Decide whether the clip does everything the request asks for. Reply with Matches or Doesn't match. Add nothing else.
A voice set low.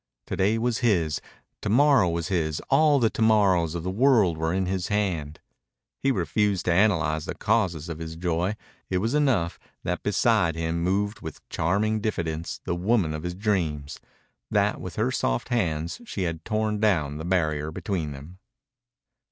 Matches